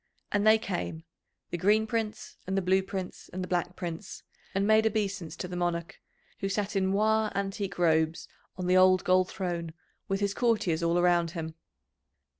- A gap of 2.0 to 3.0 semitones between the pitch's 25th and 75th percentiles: Yes, narrow, 2.6 semitones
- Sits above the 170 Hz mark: Yes, medium, 185 Hz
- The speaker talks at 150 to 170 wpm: No, average, 180 wpm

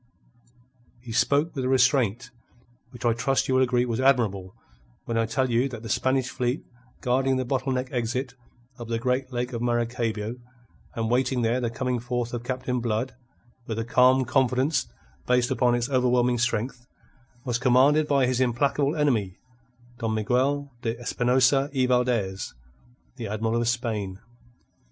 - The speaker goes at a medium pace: Yes, average, 160 wpm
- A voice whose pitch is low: Yes, low, 125 Hz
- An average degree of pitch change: No, narrow, 1.9 semitones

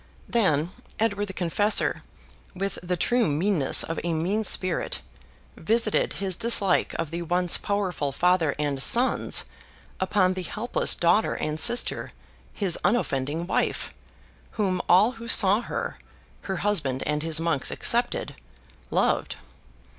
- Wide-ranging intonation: No, average, 4.1 semitones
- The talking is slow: Yes, slow, 130 wpm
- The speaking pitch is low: No, medium, 185 Hz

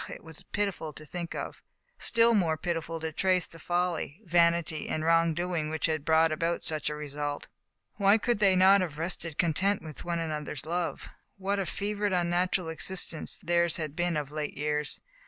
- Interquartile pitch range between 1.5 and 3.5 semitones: Yes, average, 2.7 semitones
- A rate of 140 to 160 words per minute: No, average, 180 wpm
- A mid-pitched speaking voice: Yes, medium, 170 Hz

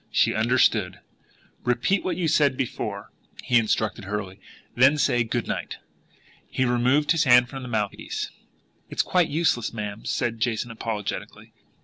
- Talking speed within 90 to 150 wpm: Yes, average, 145 wpm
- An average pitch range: Yes, average, 3.5 semitones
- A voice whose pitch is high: No, low, 120 Hz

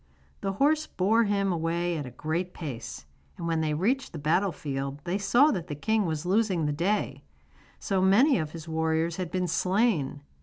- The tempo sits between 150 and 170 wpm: No, average, 190 wpm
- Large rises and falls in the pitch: No, average, 4.2 semitones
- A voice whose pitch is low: No, medium, 175 Hz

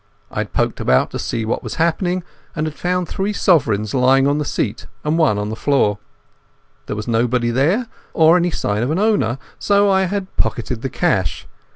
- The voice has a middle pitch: Yes, medium, 145 Hz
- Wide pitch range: Yes, wide, 7.5 semitones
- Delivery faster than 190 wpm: Yes, average, 200 wpm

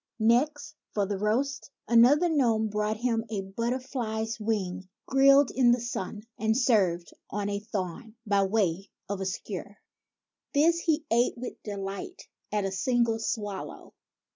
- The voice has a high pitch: Yes, high, 220 Hz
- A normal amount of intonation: Yes, average, 3.7 semitones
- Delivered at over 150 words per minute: No, average, 145 wpm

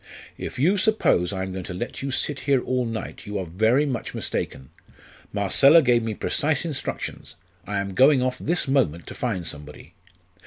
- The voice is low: Yes, low, 120 Hz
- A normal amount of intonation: No, wide, 6.4 semitones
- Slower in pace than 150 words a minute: No, average, 185 wpm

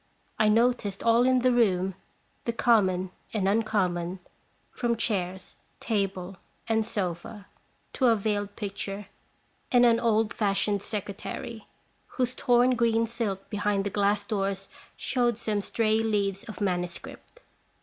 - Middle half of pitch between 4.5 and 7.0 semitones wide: No, average, 2.8 semitones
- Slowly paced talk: Yes, slow, 130 wpm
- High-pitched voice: Yes, high, 210 Hz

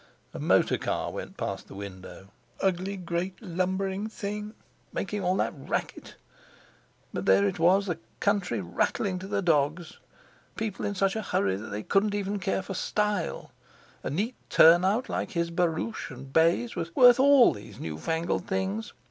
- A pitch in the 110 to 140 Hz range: No, medium, 185 Hz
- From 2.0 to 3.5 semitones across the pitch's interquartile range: No, average, 4.0 semitones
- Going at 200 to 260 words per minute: No, average, 160 wpm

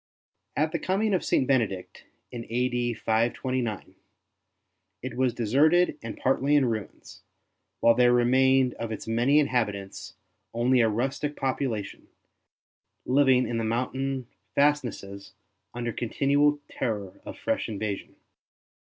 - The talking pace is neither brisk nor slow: No, slow, 120 wpm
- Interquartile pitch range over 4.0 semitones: No, average, 3.2 semitones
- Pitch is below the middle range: Yes, low, 125 Hz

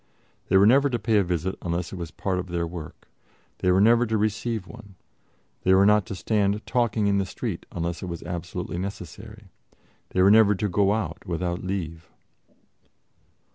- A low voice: Yes, very low, 95 Hz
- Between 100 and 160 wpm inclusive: No, average, 185 wpm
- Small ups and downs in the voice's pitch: No, average, 3.2 semitones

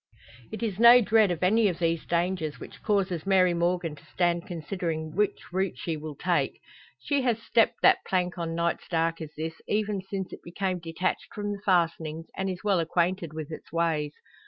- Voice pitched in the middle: Yes, medium, 175 Hz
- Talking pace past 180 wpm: Yes, average, 190 wpm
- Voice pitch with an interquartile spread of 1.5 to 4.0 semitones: Yes, average, 3.0 semitones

